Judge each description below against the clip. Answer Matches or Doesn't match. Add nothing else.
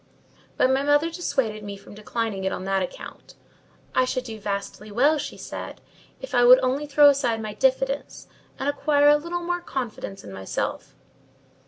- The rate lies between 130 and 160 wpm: Doesn't match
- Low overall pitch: Doesn't match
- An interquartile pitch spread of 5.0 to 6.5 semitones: Matches